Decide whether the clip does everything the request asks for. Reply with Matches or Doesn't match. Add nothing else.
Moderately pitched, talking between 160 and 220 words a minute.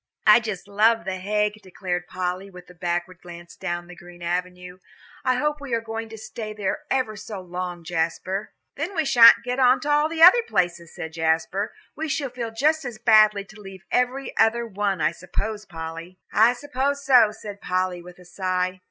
Doesn't match